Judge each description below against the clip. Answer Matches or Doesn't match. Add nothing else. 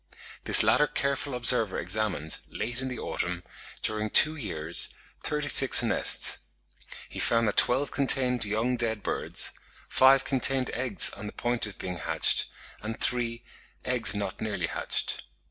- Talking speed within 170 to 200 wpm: Doesn't match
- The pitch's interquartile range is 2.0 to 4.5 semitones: Matches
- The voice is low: Matches